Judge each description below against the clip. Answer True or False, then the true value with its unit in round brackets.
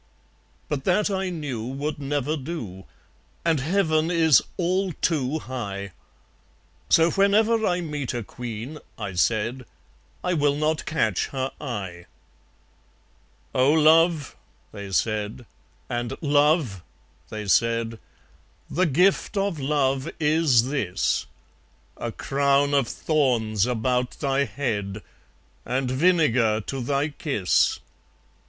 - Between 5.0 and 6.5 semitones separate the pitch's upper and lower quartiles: True (5.3 semitones)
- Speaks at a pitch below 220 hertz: True (140 Hz)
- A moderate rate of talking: False (110 wpm)